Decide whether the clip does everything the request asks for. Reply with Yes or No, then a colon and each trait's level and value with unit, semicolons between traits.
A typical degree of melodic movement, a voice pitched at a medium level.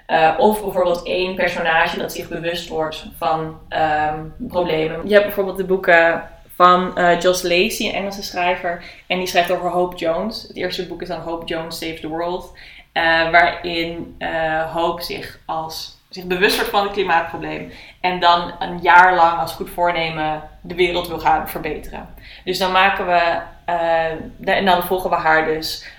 No: narrow, 1.8 semitones; medium, 175 Hz